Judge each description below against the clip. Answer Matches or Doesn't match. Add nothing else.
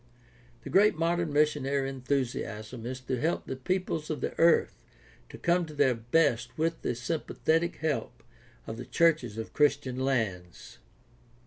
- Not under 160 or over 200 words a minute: Doesn't match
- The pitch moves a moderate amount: Matches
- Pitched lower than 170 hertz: Matches